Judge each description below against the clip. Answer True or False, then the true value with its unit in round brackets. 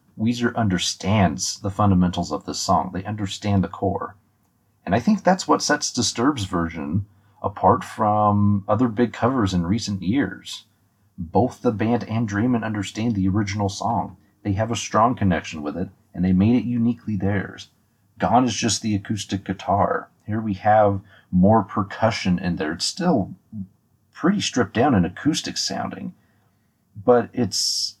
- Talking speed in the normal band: True (155 wpm)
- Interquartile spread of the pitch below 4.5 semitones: True (2.7 semitones)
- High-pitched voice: False (105 Hz)